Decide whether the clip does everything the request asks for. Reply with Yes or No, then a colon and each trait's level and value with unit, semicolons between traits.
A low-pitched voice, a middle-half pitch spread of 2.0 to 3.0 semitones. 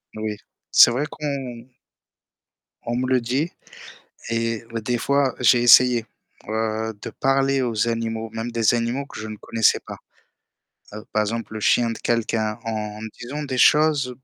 Yes: low, 115 Hz; narrow, 2.5 semitones